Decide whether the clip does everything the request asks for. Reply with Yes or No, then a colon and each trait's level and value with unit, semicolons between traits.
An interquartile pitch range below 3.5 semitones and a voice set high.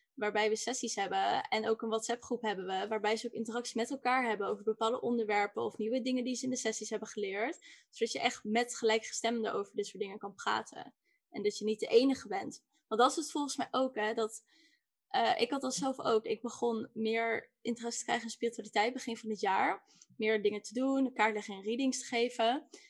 Yes: average, 2.8 semitones; high, 230 Hz